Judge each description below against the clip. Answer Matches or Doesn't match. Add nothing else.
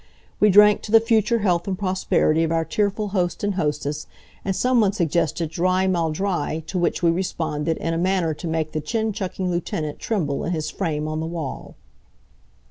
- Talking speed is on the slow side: Doesn't match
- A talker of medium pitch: Matches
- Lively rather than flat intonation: Doesn't match